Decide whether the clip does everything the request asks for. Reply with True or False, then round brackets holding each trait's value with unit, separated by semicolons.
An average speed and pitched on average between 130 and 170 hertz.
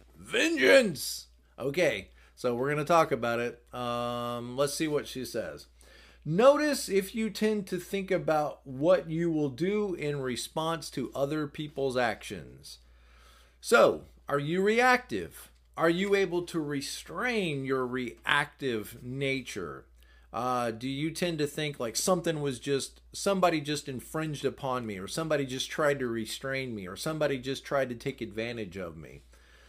True (150 wpm; 140 Hz)